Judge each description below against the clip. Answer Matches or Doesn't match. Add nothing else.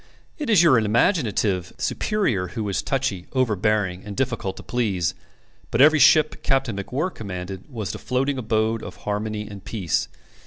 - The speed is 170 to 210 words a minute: Doesn't match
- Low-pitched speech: Matches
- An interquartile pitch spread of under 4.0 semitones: Doesn't match